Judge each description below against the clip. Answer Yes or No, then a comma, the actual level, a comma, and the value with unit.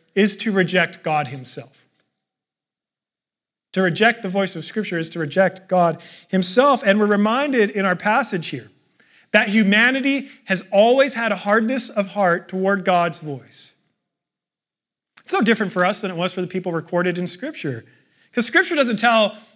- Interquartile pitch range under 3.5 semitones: No, average, 4.1 semitones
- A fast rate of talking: No, average, 165 wpm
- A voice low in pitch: No, high, 195 Hz